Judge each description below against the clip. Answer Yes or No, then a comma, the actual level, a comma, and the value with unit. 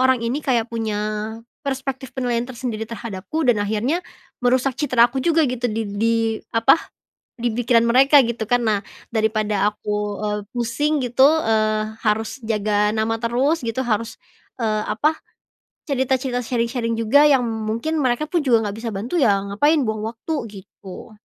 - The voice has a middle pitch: No, high, 230 Hz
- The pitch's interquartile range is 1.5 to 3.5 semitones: Yes, average, 3.2 semitones